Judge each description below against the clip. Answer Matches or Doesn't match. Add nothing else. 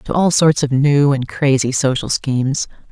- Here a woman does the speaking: Matches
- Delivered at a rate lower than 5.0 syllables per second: Matches